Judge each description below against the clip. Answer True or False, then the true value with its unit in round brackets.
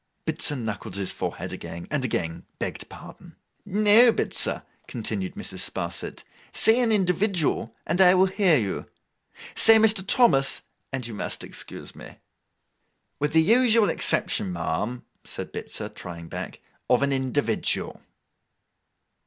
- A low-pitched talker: False (145 Hz)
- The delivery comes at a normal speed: False (130 wpm)